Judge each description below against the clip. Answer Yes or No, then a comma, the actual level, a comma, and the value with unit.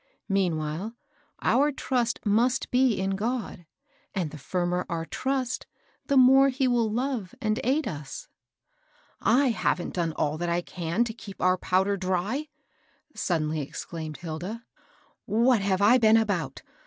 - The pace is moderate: Yes, average, 150 wpm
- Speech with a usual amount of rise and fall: No, wide, 6.1 semitones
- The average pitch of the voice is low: No, high, 205 Hz